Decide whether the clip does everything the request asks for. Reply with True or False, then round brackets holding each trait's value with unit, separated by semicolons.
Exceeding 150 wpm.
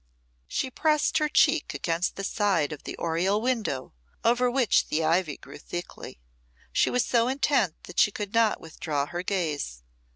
True (165 wpm)